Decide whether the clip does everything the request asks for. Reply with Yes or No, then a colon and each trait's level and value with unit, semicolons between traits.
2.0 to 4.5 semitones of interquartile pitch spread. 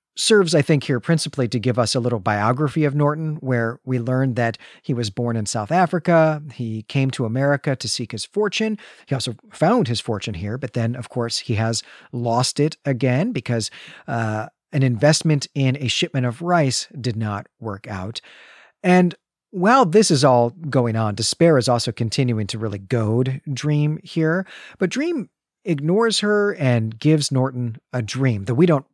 No: average, 4.9 semitones